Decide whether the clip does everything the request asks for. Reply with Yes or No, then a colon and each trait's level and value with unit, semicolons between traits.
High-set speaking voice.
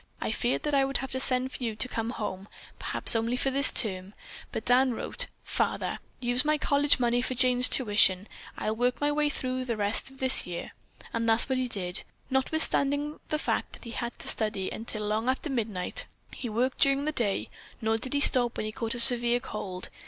Yes: high, 245 Hz